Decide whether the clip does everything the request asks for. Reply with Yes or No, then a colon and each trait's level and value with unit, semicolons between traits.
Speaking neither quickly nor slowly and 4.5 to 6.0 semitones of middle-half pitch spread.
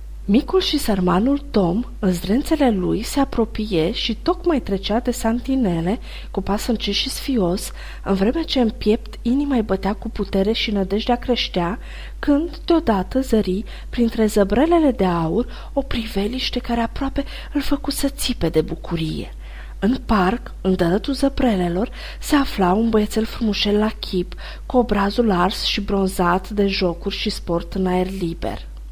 Yes: average, 150 wpm; average, 4.8 semitones